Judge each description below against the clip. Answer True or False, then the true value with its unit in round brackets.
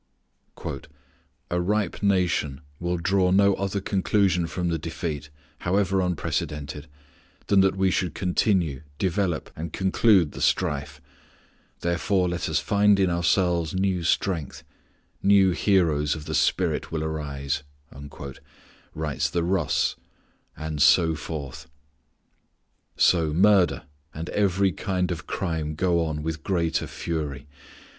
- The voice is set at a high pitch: False (85 Hz)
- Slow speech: True (120 wpm)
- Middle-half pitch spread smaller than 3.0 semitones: False (3.4 semitones)